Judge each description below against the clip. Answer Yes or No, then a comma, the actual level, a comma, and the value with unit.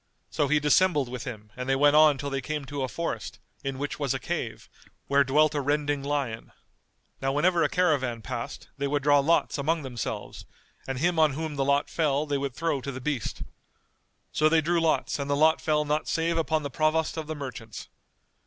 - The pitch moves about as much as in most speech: No, narrow, 2.3 semitones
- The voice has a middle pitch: Yes, medium, 145 Hz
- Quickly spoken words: Yes, fast, 210 wpm